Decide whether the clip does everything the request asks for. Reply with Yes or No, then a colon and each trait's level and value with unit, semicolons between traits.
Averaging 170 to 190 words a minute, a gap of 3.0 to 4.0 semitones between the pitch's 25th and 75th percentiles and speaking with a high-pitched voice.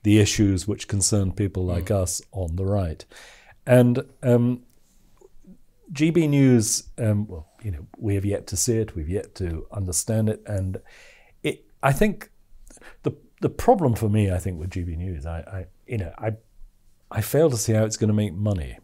No: average, 185 wpm; average, 3.7 semitones; low, 105 Hz